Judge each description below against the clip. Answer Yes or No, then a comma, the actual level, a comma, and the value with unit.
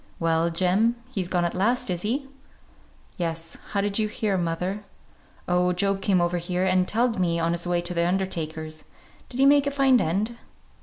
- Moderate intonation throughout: Yes, average, 3.7 semitones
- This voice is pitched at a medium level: Yes, medium, 180 Hz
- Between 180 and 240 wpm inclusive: Yes, average, 190 wpm